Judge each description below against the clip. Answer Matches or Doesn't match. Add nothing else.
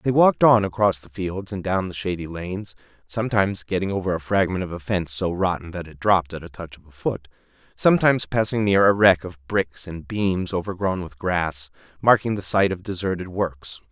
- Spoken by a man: Matches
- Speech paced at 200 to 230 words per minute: Matches